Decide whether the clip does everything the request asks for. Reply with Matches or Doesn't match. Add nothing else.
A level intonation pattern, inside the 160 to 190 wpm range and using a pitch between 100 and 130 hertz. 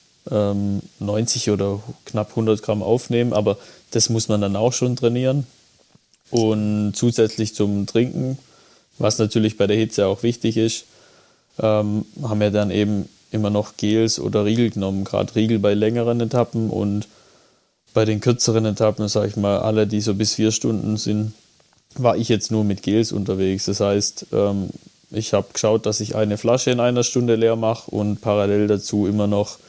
Matches